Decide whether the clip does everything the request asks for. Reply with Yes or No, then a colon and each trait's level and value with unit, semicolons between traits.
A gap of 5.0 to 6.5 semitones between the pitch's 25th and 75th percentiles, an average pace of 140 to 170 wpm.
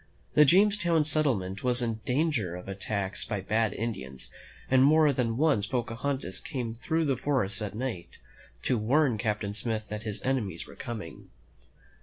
Yes: wide, 5.4 semitones; average, 165 wpm